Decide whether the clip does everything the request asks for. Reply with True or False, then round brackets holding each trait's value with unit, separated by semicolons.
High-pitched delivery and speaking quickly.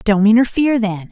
False (220 Hz; 160 wpm)